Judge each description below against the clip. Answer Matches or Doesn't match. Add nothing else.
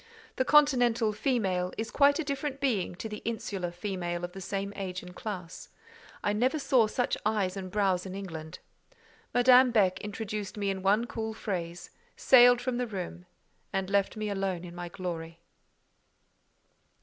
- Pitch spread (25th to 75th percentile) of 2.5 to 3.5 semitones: Doesn't match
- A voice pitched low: Doesn't match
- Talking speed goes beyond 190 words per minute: Doesn't match